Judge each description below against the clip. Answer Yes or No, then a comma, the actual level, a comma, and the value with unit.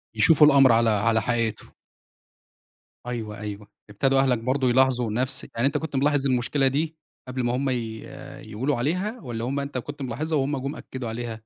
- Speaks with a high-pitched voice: No, low, 130 Hz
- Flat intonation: No, average, 3.2 semitones